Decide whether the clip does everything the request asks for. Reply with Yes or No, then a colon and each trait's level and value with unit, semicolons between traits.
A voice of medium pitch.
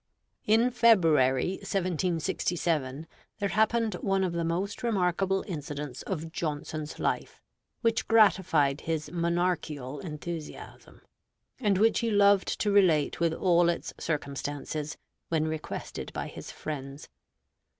Yes: medium, 170 Hz